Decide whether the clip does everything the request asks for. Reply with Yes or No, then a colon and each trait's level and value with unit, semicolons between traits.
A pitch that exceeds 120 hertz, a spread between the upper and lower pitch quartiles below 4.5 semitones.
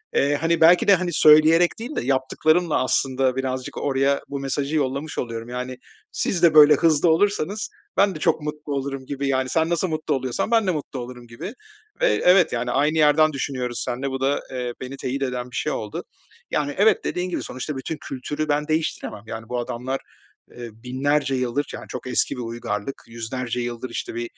Yes: medium, 140 Hz; average, 3.7 semitones